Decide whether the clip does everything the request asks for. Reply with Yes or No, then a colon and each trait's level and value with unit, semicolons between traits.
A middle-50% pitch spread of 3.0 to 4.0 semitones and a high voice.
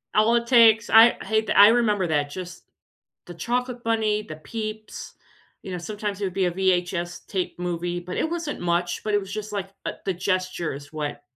Yes: average, 3.7 semitones; high, 195 Hz